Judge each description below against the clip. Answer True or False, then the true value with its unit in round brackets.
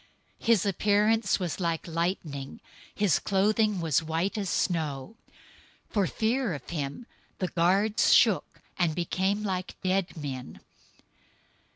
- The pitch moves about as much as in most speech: True (4.1 semitones)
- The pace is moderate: False (130 wpm)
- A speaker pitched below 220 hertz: True (185 Hz)